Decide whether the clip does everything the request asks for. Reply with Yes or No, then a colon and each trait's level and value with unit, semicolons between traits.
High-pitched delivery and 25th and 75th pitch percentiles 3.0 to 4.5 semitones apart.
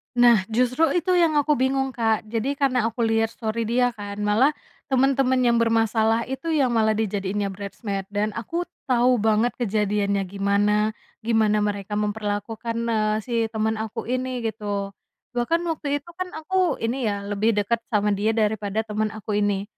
Yes: high, 225 Hz; average, 3.3 semitones